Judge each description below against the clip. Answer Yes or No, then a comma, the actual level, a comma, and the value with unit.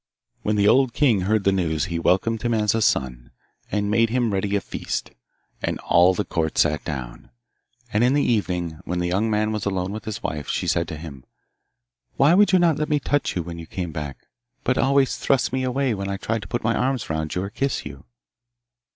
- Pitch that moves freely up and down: Yes, wide, 5.7 semitones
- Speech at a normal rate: No, fast, 220 wpm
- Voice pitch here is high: No, low, 100 Hz